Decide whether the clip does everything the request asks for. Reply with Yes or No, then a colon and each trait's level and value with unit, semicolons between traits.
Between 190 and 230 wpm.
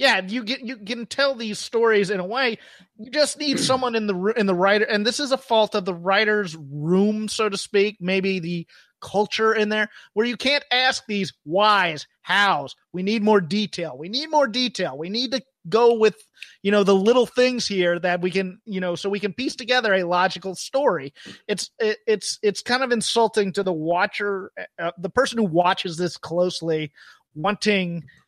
Yes: average, 195 wpm